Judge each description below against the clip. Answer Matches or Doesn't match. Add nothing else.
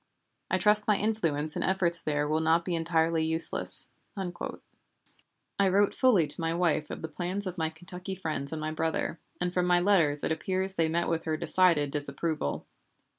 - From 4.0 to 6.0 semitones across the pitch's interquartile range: Doesn't match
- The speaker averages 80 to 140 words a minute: Doesn't match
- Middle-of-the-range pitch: Matches